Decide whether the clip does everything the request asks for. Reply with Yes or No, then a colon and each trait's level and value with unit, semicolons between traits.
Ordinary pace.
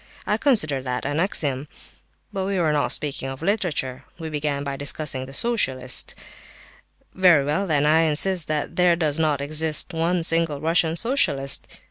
Yes: average, 160 wpm